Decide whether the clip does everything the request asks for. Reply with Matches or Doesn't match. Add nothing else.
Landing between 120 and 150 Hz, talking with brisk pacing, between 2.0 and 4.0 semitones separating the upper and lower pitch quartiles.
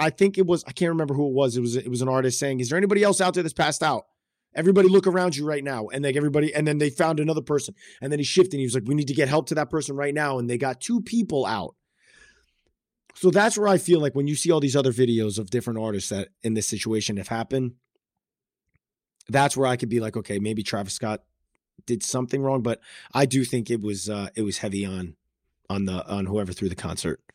Doesn't match